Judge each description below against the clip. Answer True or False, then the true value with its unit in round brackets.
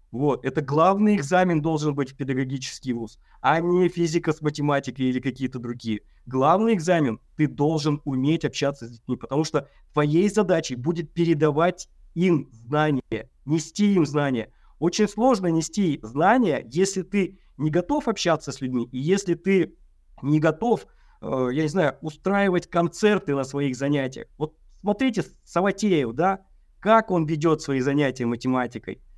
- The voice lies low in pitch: False (155 Hz)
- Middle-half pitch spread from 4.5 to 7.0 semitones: True (5.1 semitones)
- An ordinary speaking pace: True (145 wpm)